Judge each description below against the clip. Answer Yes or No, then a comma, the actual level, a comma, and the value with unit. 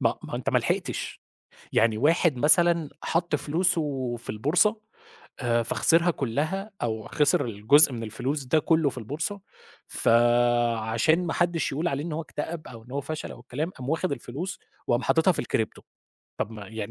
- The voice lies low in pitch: No, medium, 145 Hz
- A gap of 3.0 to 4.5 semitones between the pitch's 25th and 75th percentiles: No, wide, 5.5 semitones